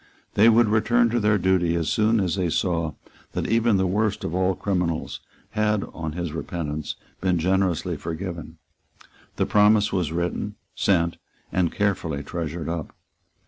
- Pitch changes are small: No, average, 3.8 semitones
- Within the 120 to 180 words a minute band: Yes, average, 150 wpm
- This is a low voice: Yes, very low, 90 Hz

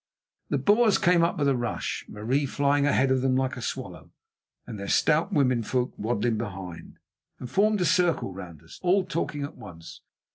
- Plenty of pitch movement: Yes, wide, 6.7 semitones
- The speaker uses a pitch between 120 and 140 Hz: Yes, low, 135 Hz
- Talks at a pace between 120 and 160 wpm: No, average, 180 wpm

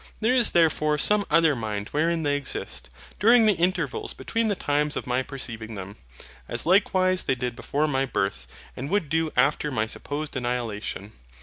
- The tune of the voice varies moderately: No, wide, 5.7 semitones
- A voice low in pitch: No, medium, 145 Hz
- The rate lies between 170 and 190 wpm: Yes, average, 175 wpm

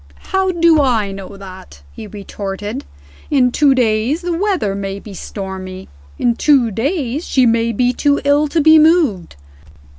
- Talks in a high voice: Yes, high, 240 Hz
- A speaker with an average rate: Yes, average, 155 wpm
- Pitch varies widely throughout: Yes, wide, 7.1 semitones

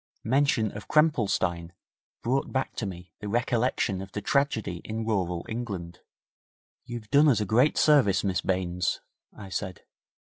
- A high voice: No, low, 105 Hz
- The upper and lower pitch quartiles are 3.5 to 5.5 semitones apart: Yes, average, 5.2 semitones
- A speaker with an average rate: Yes, average, 145 wpm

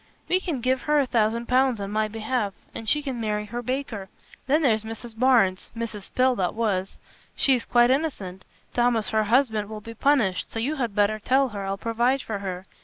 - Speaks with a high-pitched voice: Yes, high, 230 Hz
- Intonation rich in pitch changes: No, average, 3.6 semitones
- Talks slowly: No, fast, 205 wpm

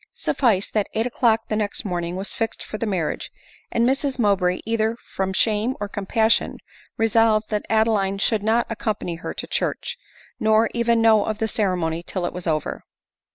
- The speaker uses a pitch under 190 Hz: No, high, 215 Hz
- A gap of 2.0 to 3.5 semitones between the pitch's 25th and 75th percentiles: Yes, average, 2.8 semitones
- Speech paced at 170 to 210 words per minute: Yes, average, 180 wpm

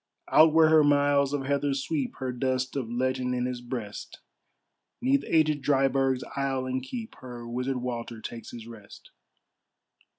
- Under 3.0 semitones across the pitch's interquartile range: Yes, narrow, 2.4 semitones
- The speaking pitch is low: Yes, low, 130 Hz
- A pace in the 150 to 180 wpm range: Yes, average, 155 wpm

